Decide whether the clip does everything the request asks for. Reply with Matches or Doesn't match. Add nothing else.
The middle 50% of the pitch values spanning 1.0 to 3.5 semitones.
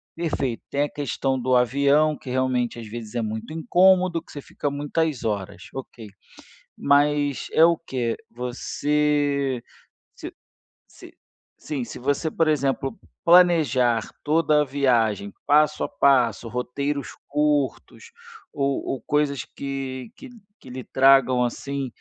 Matches